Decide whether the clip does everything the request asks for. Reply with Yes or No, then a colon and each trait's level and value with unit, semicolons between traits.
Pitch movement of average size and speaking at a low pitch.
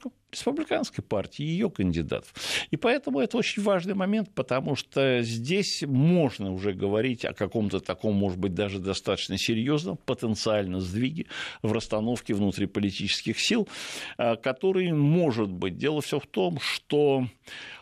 No: wide, 8.5 semitones; low, 125 Hz